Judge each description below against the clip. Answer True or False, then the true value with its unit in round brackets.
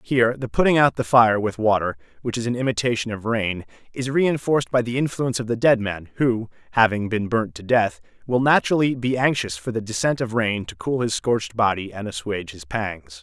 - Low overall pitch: True (115 Hz)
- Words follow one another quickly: True (215 wpm)